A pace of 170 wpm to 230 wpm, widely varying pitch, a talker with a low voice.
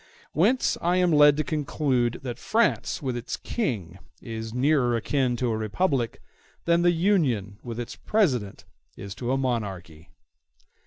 No: average, 150 wpm; wide, 5.7 semitones; low, 125 Hz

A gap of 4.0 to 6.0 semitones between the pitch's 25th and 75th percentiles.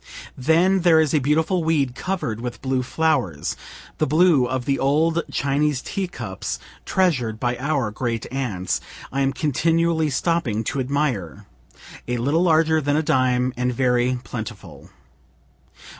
Yes: average, 4.5 semitones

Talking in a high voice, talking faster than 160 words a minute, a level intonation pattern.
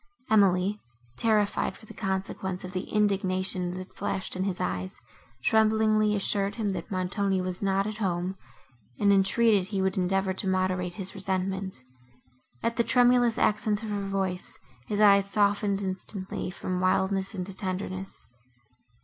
No: high, 195 Hz; average, 145 wpm; narrow, 1.8 semitones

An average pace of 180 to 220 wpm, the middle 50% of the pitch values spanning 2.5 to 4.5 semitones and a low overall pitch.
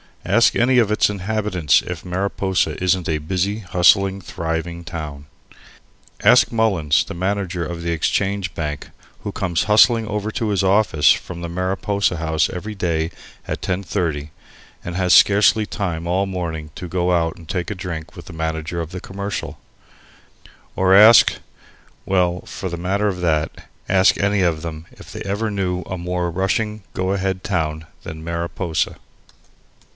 No: average, 160 wpm; average, 3.0 semitones; very low, 90 Hz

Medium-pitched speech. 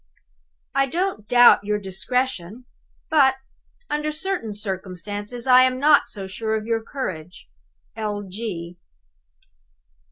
No: high, 225 Hz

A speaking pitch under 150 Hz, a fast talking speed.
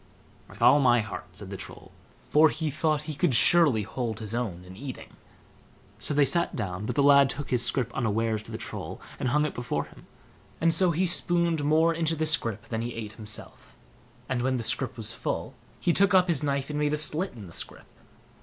Yes: medium, 140 Hz; fast, 220 wpm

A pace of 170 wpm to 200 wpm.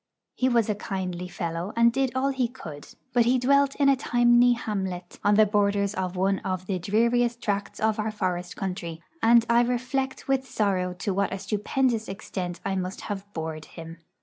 Yes: average, 190 wpm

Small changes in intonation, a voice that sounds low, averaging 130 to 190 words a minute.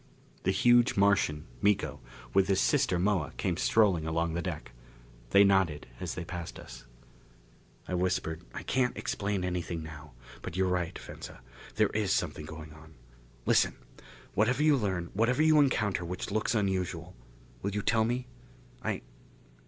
No: average, 4.0 semitones; very low, 95 Hz; average, 155 wpm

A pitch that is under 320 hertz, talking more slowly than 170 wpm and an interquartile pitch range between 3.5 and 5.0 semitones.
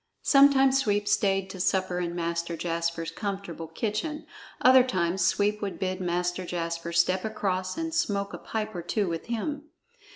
Yes: high, 190 Hz; average, 160 wpm; average, 3.9 semitones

